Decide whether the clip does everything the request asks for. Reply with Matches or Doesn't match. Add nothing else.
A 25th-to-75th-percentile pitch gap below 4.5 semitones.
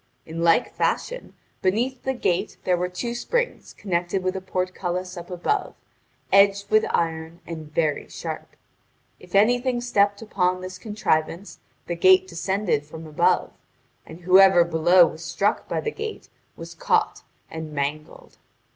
Matches